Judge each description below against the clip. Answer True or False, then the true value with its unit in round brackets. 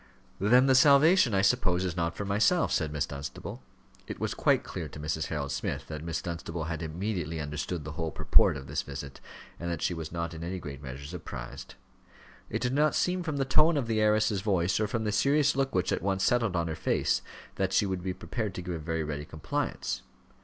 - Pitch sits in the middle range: False (90 Hz)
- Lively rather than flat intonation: True (5.7 semitones)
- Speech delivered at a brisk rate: True (225 wpm)